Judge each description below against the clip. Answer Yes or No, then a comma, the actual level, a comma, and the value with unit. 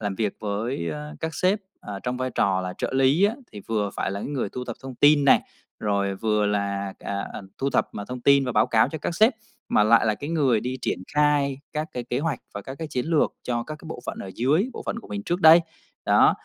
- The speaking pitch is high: No, low, 125 Hz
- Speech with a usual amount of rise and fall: No, wide, 6.3 semitones